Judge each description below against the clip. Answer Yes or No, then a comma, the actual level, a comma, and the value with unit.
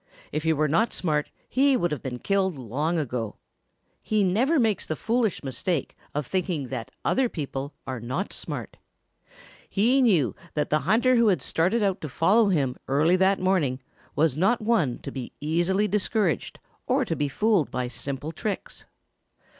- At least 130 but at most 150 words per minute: No, average, 170 wpm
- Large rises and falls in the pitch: Yes, wide, 6.7 semitones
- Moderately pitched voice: Yes, medium, 170 Hz